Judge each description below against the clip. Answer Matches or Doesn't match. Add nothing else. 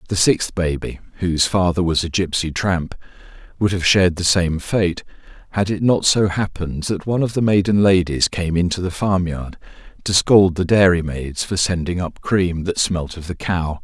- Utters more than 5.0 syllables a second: Doesn't match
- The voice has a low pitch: Matches